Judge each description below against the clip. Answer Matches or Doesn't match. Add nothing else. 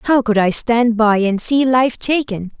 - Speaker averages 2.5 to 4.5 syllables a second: Matches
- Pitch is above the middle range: Matches